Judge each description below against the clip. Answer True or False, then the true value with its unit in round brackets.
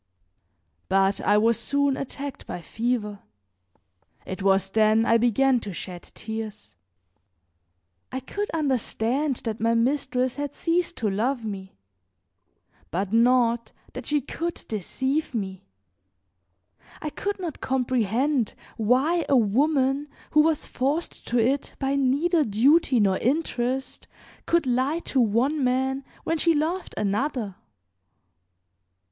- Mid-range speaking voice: False (255 Hz)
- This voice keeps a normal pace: False (120 wpm)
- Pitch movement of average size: True (4.5 semitones)